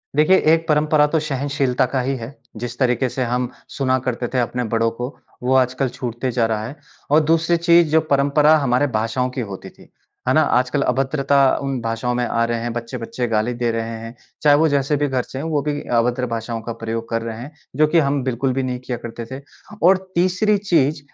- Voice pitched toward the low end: Yes, low, 130 Hz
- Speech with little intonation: No, average, 3.5 semitones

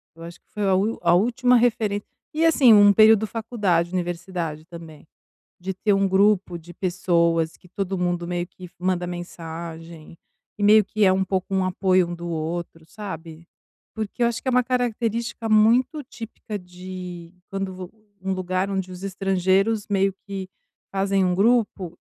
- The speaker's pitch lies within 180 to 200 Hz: Yes, high, 190 Hz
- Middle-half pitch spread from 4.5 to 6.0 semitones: No, average, 3.4 semitones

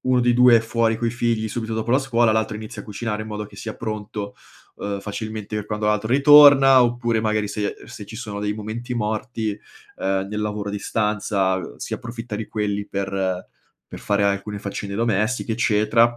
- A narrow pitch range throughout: Yes, narrow, 2.1 semitones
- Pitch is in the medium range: No, low, 110 Hz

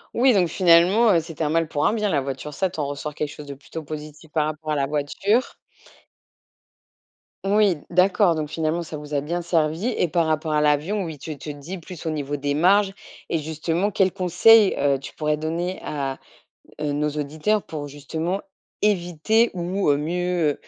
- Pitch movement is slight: No, average, 3.4 semitones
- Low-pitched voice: No, medium, 160 Hz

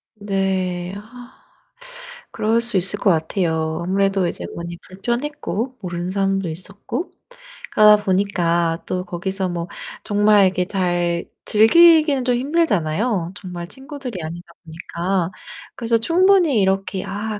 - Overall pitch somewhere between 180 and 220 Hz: Yes, high, 195 Hz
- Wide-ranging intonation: No, average, 4.6 semitones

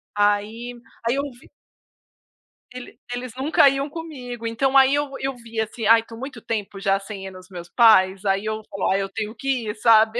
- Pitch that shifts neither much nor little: Yes, average, 3.7 semitones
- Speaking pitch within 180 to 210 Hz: No, high, 230 Hz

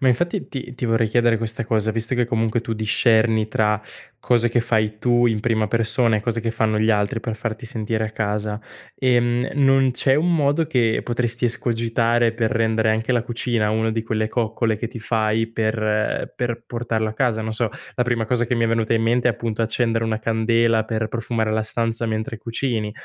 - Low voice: Yes, low, 115 Hz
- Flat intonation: Yes, narrow, 1.5 semitones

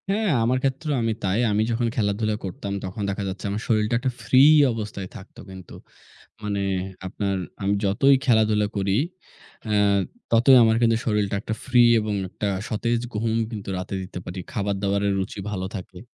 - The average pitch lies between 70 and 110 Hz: Yes, low, 105 Hz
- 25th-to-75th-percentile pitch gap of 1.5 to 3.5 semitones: Yes, average, 2.7 semitones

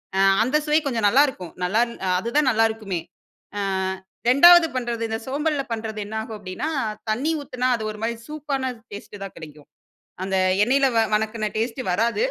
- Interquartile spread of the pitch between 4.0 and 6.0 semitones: Yes, average, 4.3 semitones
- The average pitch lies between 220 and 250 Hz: Yes, high, 230 Hz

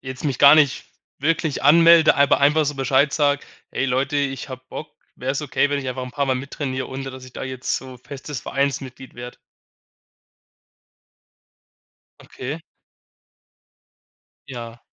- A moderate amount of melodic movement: No, narrow, 1.8 semitones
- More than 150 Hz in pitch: No, low, 135 Hz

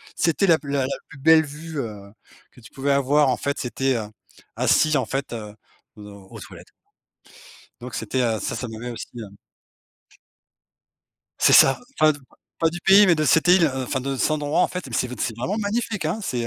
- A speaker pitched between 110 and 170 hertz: Yes, medium, 140 Hz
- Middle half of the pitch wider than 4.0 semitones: Yes, average, 4.9 semitones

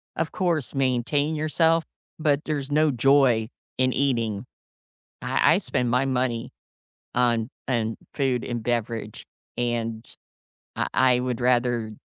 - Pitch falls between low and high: No, low, 125 Hz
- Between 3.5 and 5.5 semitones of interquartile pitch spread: No, average, 3.1 semitones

